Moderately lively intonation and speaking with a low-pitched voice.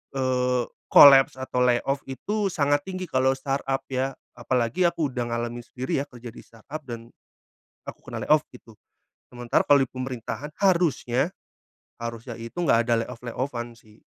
Yes: average, 3.0 semitones; low, 130 Hz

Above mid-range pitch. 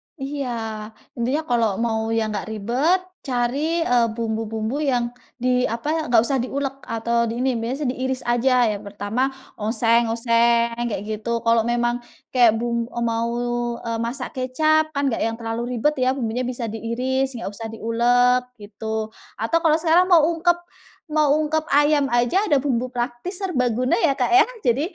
Yes: high, 240 Hz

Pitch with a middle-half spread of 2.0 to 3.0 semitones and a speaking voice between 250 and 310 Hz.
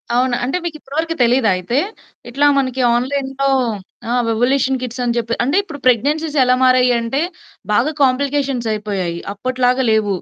Yes: average, 2.7 semitones; very high, 255 Hz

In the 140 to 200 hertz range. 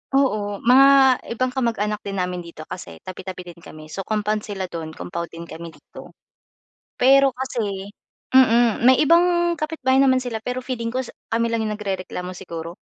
No: high, 220 Hz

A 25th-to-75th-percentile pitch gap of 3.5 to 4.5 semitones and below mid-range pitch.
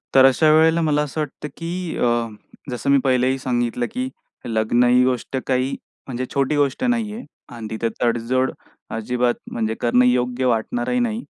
Yes: average, 3.9 semitones; low, 130 Hz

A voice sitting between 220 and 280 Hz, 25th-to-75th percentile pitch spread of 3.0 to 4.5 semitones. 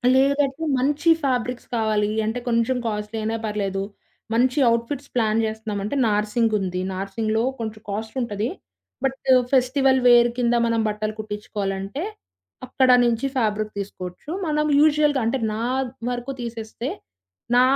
Yes: high, 230 Hz; average, 3.4 semitones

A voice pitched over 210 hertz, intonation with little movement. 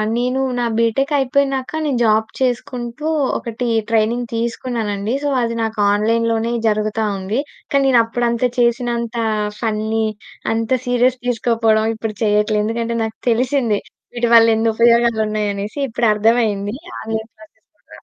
Yes: high, 230 Hz; narrow, 1.7 semitones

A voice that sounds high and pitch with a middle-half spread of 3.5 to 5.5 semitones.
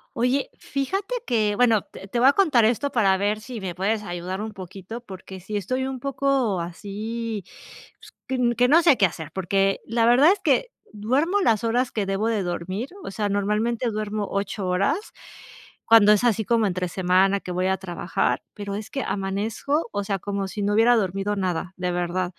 Yes: high, 210 Hz; average, 3.8 semitones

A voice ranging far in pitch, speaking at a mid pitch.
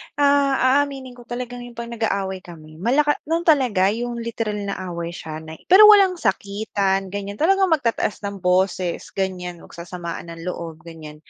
No: wide, 6.3 semitones; high, 200 Hz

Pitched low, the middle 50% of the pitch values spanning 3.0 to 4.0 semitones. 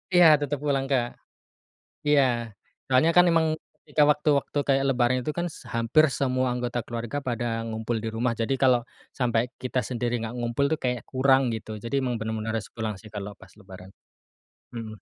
Yes: low, 125 Hz; average, 3.3 semitones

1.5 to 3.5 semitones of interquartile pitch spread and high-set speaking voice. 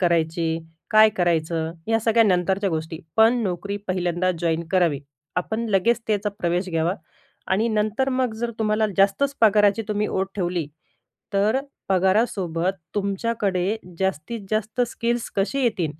No: average, 4.0 semitones; high, 195 Hz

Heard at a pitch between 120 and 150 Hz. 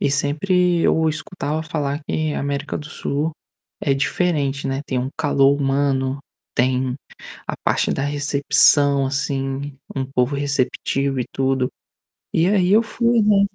Yes: medium, 140 Hz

